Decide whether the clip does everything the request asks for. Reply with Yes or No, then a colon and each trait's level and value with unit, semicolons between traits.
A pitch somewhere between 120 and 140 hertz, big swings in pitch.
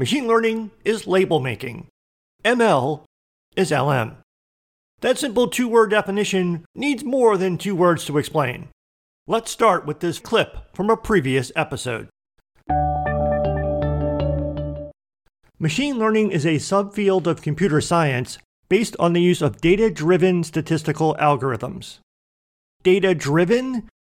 No: medium, 165 Hz; wide, 8.1 semitones